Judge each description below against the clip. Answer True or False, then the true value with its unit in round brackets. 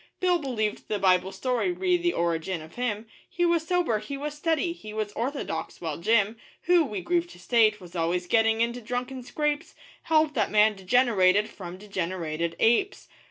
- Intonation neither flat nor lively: False (7.7 semitones)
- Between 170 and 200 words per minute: True (175 wpm)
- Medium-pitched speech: False (225 Hz)